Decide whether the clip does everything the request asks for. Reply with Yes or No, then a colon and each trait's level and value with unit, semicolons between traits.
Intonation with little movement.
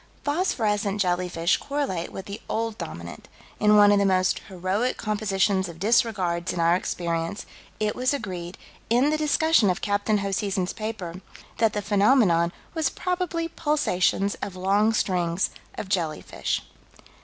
No: average, 3.9 semitones